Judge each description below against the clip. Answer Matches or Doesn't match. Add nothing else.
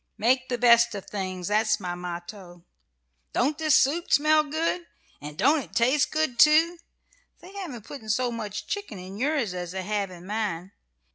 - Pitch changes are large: Matches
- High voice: Matches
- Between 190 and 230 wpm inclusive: Doesn't match